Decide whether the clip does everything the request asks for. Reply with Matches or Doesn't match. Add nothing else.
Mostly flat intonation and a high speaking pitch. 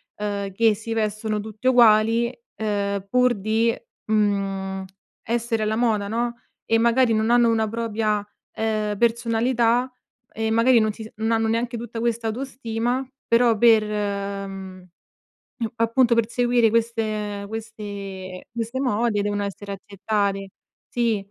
Matches